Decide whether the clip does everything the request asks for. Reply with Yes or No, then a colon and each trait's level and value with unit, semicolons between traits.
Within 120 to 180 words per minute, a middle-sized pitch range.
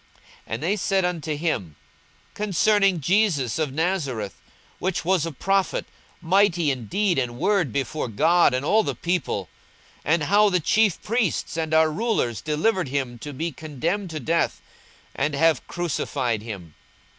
No: average, 155 wpm; wide, 5.8 semitones